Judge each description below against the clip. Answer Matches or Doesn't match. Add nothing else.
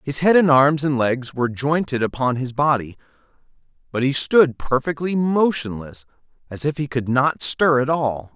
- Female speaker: Doesn't match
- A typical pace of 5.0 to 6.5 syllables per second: Doesn't match